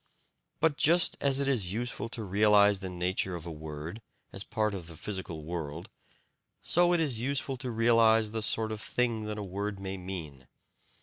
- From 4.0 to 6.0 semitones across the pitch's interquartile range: Yes, average, 4.5 semitones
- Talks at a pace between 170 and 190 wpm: Yes, average, 185 wpm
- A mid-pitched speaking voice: No, low, 105 Hz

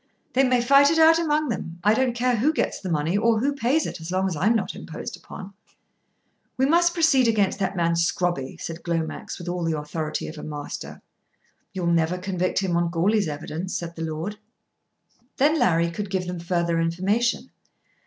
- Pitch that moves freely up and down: Yes, wide, 6.3 semitones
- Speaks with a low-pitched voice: No, medium, 185 Hz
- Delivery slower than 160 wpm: No, average, 195 wpm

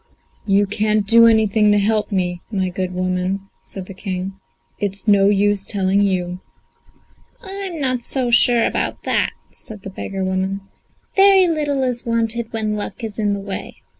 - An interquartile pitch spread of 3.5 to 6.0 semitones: No, average, 3.1 semitones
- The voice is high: Yes, high, 205 Hz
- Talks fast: No, average, 165 wpm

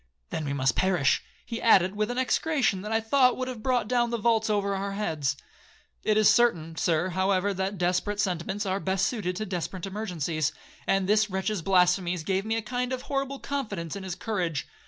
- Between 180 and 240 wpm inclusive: Yes, average, 200 wpm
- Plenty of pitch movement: No, average, 3.7 semitones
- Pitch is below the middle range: No, high, 195 Hz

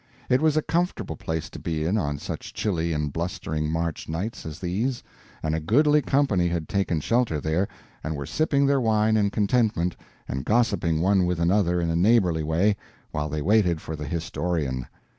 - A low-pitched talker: Yes, very low, 90 Hz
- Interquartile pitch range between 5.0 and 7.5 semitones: Yes, wide, 5.5 semitones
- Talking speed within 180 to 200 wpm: Yes, average, 185 wpm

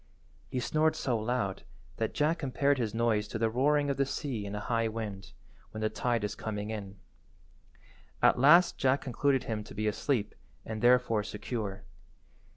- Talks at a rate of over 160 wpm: Yes, average, 170 wpm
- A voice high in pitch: No, low, 115 Hz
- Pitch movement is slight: No, average, 3.9 semitones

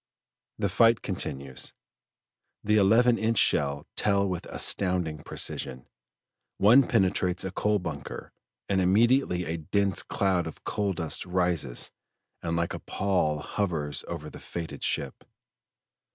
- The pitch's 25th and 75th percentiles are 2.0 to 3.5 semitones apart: No, average, 4.0 semitones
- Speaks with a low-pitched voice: Yes, very low, 90 Hz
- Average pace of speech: No, slow, 125 wpm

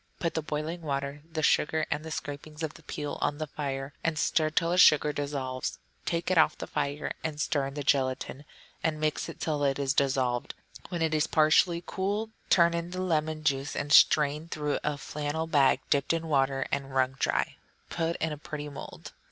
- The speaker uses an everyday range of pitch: No, narrow, 2.3 semitones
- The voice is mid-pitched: Yes, medium, 150 Hz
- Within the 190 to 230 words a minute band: Yes, average, 200 wpm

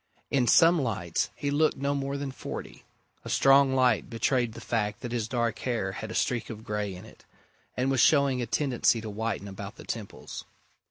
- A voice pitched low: Yes, low, 120 Hz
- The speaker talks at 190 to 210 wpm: Yes, average, 200 wpm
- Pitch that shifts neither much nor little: Yes, average, 4.0 semitones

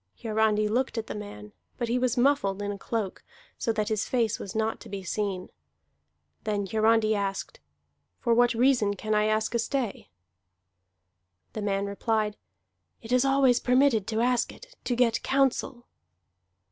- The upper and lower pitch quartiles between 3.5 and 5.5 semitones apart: No, average, 2.9 semitones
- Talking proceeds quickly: No, average, 160 wpm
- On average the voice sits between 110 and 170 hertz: No, high, 220 Hz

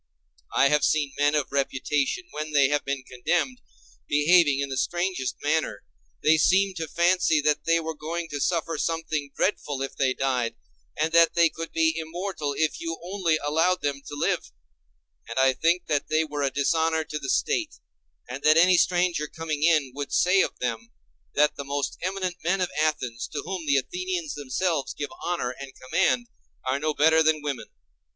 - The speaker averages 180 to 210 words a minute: Yes, average, 185 wpm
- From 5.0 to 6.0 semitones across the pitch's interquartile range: No, average, 3.2 semitones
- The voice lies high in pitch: No, medium, 155 Hz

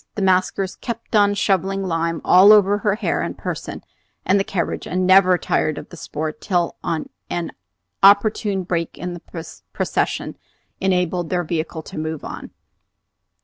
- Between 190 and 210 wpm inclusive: No, average, 150 wpm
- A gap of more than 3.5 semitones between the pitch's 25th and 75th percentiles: No, average, 2.7 semitones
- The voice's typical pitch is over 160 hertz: Yes, medium, 185 Hz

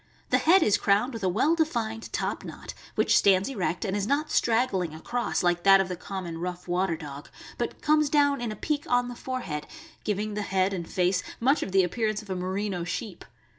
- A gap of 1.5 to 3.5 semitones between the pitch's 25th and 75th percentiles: No, average, 5.1 semitones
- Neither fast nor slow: No, fast, 215 wpm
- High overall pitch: Yes, high, 200 Hz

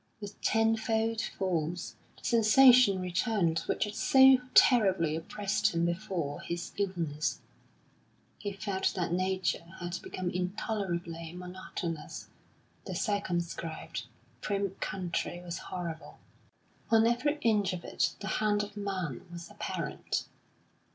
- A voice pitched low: No, medium, 185 Hz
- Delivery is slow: Yes, slow, 115 wpm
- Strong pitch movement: No, average, 3.6 semitones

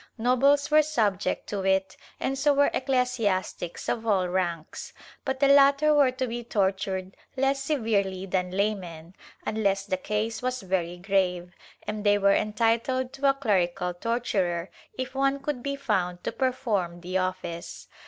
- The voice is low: No, high, 210 Hz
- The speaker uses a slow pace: No, average, 155 wpm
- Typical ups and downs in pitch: No, wide, 5.9 semitones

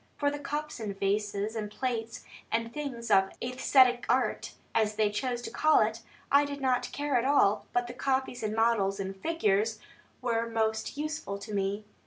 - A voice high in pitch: Yes, high, 230 Hz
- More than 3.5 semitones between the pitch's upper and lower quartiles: Yes, average, 3.9 semitones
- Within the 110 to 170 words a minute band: No, average, 180 wpm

